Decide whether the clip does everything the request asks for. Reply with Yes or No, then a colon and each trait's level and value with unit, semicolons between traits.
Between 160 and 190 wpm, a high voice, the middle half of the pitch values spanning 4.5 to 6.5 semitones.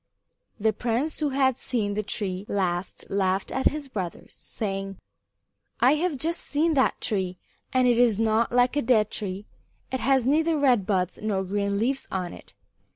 Yes: average, 170 wpm; high, 225 Hz; average, 5.2 semitones